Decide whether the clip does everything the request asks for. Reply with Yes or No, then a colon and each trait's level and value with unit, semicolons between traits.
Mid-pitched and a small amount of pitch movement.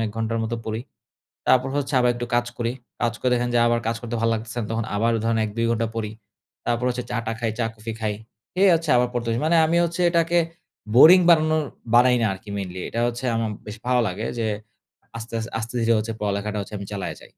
No: low, 115 Hz; narrow, 1.9 semitones